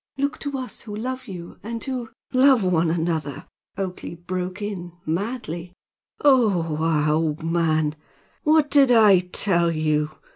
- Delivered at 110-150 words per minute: Yes, average, 145 wpm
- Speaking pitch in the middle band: Yes, medium, 180 Hz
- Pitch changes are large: Yes, wide, 6.5 semitones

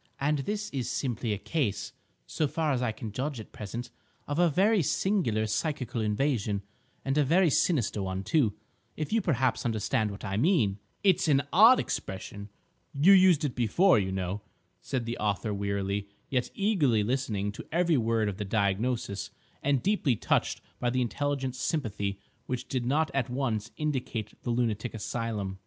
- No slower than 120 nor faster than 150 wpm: No, average, 170 wpm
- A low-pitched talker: Yes, low, 125 Hz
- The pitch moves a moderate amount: No, wide, 6.0 semitones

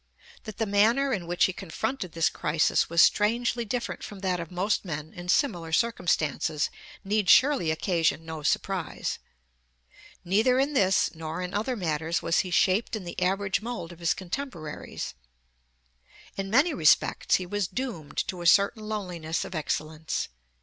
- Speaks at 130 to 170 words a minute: Yes, average, 155 wpm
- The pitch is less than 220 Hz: Yes, medium, 185 Hz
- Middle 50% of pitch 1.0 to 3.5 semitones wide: No, average, 4.6 semitones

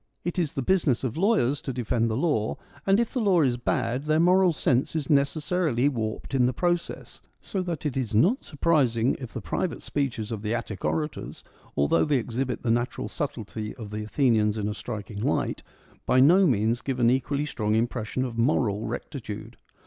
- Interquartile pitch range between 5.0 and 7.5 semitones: Yes, average, 5.3 semitones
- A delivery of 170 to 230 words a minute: Yes, average, 190 wpm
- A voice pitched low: Yes, low, 130 Hz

